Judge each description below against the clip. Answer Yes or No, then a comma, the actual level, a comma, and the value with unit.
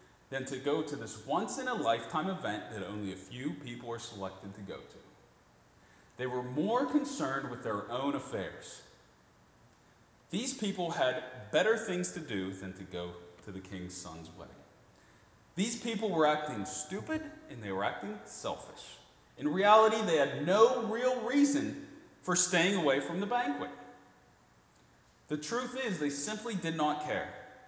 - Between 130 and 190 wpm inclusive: Yes, average, 160 wpm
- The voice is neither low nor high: Yes, medium, 150 Hz